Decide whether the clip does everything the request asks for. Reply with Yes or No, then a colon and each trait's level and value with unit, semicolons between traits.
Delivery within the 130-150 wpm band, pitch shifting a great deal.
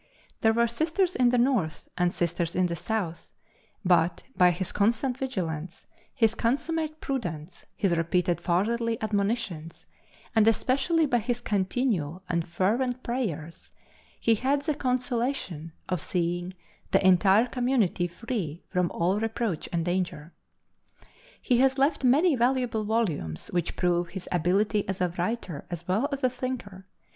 Yes: average, 140 wpm; wide, 6.1 semitones